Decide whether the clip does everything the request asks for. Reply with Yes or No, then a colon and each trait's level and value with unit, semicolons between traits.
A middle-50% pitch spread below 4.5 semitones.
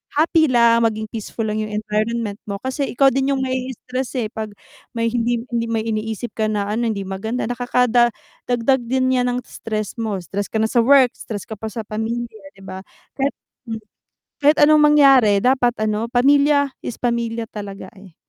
Yes: average, 2.9 semitones